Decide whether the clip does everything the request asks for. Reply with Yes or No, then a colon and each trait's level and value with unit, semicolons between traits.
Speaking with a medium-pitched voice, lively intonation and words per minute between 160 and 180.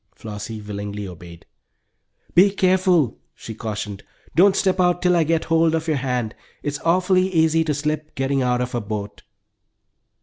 Yes: medium, 145 Hz; wide, 7.9 semitones; average, 165 wpm